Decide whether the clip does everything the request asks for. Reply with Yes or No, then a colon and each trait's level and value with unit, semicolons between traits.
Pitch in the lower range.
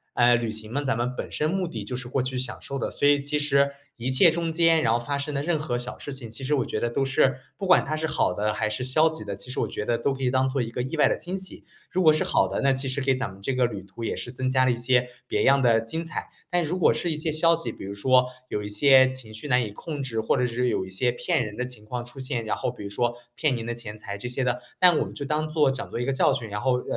Yes: low, 130 Hz